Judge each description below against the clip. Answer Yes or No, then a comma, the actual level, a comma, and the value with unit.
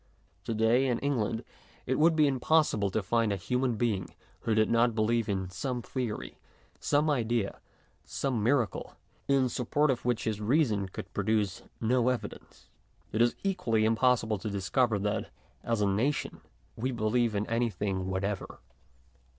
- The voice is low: Yes, low, 115 Hz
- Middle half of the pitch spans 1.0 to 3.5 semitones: Yes, average, 3.2 semitones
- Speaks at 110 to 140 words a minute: No, average, 150 wpm